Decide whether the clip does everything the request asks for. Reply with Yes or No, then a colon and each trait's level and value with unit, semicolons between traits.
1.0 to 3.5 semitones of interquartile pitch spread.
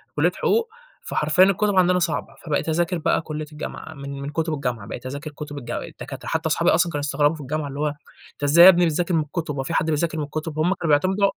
Yes: average, 2.9 semitones